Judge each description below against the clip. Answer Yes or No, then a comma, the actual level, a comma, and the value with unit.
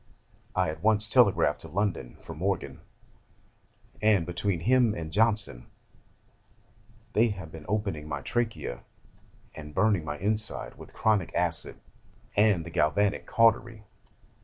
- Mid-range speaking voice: No, low, 100 Hz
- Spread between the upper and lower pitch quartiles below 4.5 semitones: No, average, 5.2 semitones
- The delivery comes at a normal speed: No, slow, 125 wpm